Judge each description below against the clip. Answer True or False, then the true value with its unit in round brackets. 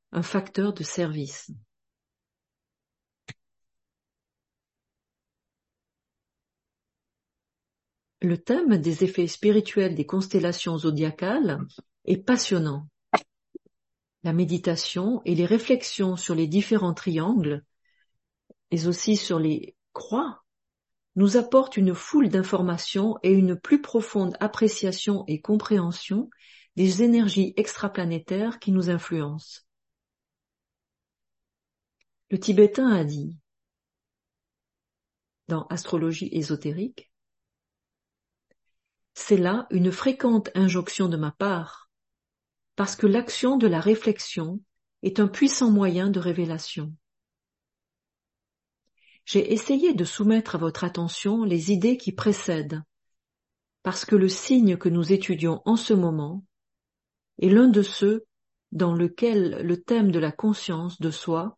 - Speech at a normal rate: False (105 wpm)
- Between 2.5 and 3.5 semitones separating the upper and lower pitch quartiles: False (4.1 semitones)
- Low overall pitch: False (185 Hz)